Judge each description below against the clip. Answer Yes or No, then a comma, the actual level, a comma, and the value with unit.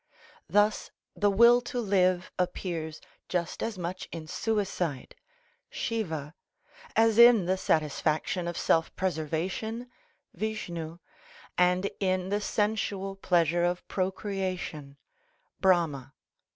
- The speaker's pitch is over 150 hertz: Yes, medium, 185 Hz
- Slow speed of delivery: Yes, slow, 100 wpm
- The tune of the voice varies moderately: Yes, average, 3.7 semitones